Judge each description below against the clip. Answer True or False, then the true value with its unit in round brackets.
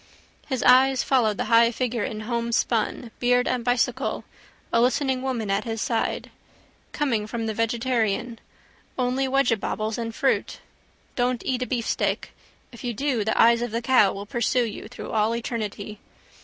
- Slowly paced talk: False (155 wpm)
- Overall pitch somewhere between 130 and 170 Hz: False (235 Hz)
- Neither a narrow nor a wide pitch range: False (2.1 semitones)